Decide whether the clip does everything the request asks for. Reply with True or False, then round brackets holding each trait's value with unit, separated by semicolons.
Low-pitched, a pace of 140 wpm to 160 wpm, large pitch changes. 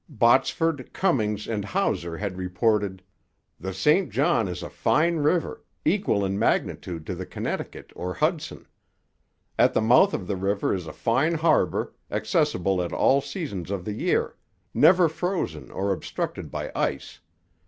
True (105 Hz; 150 wpm; 8.7 semitones)